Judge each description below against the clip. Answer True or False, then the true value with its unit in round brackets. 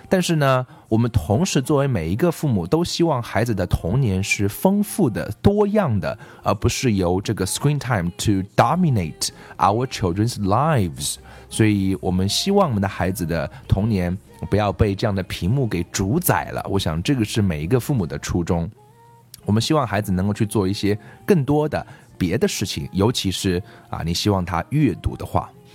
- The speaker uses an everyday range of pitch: False (6.2 semitones)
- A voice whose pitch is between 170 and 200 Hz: False (110 Hz)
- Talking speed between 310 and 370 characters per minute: True (330 characters per minute)